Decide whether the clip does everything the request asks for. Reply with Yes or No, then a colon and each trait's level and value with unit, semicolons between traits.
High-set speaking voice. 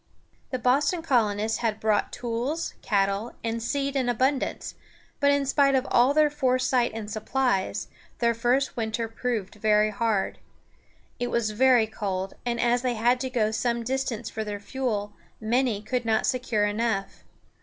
Yes: high, 235 Hz